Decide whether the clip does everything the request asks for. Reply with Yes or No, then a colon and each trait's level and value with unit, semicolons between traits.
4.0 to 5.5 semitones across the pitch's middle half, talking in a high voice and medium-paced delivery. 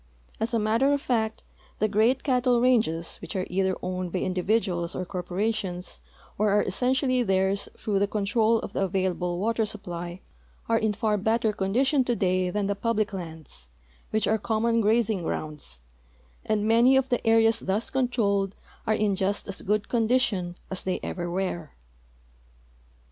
No: average, 3.6 semitones; high, 210 Hz; average, 160 wpm